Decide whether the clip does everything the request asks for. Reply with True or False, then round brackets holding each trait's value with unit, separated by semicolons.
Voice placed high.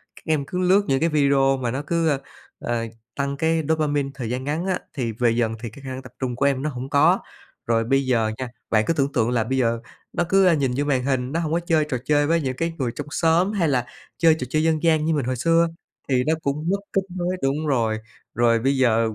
False (140 Hz)